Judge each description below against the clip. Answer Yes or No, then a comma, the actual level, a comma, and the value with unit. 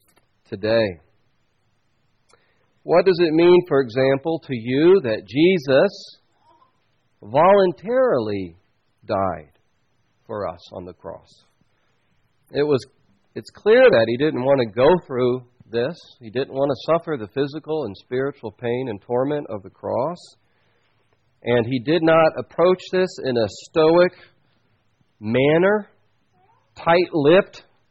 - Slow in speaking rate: Yes, slow, 120 wpm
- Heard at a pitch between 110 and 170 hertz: Yes, low, 135 Hz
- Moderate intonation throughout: No, wide, 5.8 semitones